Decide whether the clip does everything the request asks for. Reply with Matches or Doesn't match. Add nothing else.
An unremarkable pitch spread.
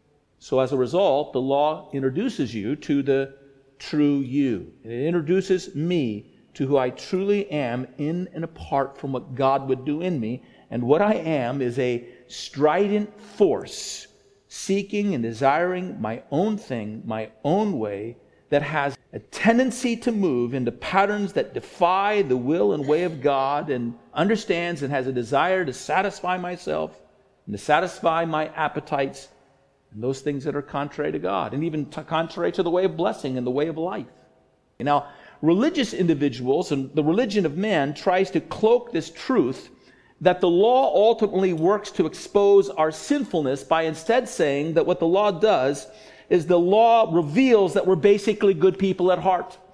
Doesn't match